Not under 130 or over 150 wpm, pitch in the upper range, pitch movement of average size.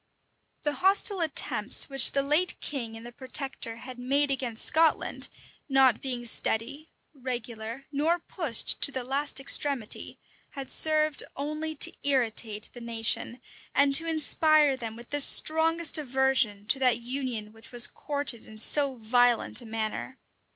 Yes: average, 145 wpm; very high, 265 Hz; average, 3.7 semitones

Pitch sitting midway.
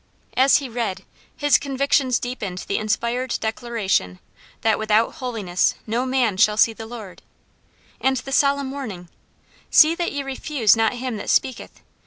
No: high, 240 Hz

